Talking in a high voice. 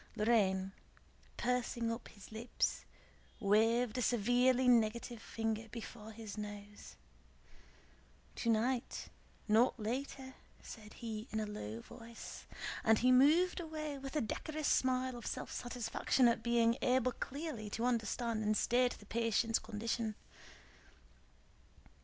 Yes: high, 230 Hz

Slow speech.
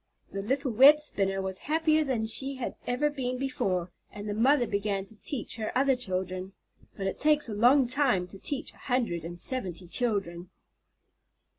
No: average, 175 wpm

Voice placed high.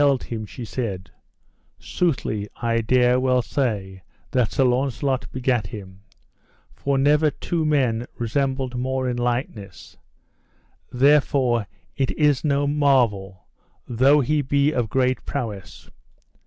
No: low, 125 Hz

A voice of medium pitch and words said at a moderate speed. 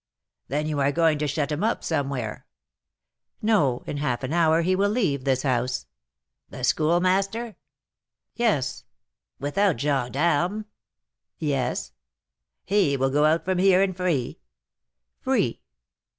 No: medium, 155 Hz; slow, 130 wpm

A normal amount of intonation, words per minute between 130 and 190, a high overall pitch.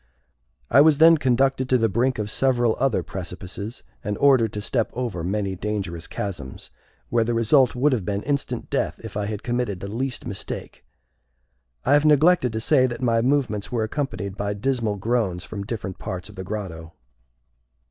No: average, 4.5 semitones; average, 180 wpm; low, 115 Hz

